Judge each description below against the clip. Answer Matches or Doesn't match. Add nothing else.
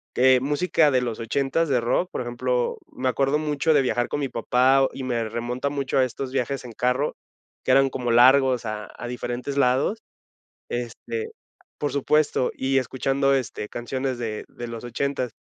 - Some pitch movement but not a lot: Doesn't match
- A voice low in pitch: Matches